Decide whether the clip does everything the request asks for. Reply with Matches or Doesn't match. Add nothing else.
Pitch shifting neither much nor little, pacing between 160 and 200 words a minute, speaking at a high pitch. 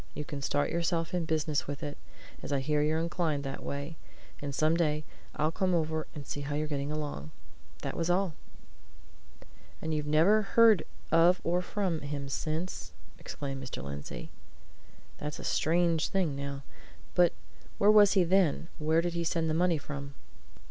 Doesn't match